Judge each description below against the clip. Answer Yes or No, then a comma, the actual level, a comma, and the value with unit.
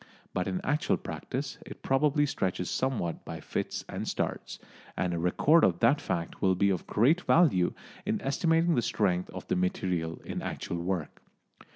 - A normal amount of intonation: No, wide, 8.4 semitones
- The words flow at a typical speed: Yes, average, 170 wpm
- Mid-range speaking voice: No, low, 100 Hz